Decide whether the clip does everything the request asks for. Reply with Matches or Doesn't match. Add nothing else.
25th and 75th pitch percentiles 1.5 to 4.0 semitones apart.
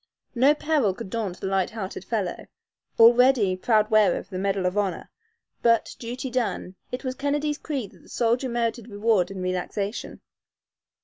Doesn't match